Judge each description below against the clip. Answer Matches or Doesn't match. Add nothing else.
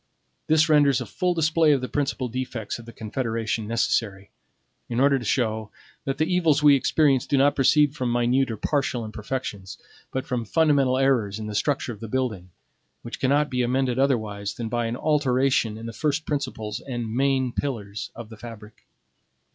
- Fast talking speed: Doesn't match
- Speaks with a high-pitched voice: Doesn't match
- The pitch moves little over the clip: Doesn't match